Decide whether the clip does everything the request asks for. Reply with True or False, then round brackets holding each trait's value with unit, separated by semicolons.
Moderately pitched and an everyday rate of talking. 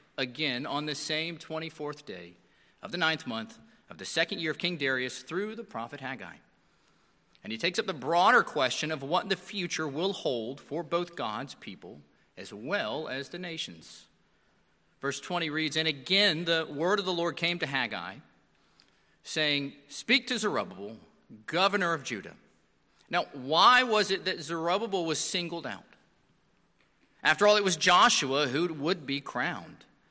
True (160 Hz; 165 wpm)